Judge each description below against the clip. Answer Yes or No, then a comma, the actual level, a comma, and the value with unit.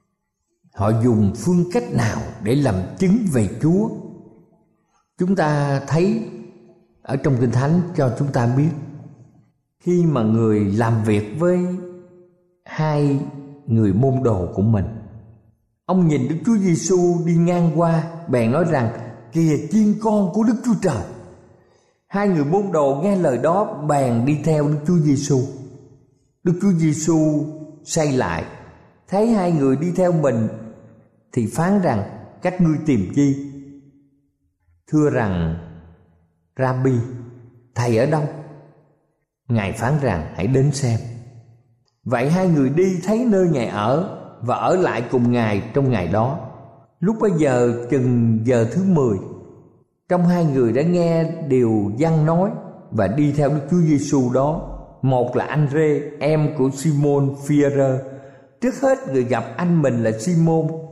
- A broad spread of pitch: Yes, wide, 5.8 semitones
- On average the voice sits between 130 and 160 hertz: Yes, medium, 140 Hz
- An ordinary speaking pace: No, slow, 145 wpm